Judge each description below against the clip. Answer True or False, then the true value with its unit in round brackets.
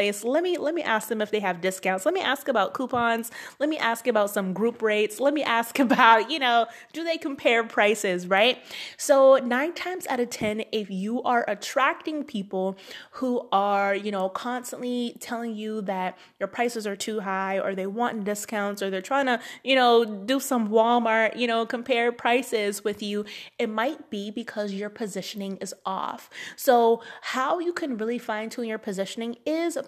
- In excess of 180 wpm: True (190 wpm)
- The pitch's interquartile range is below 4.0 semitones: True (3.6 semitones)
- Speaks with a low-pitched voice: False (230 Hz)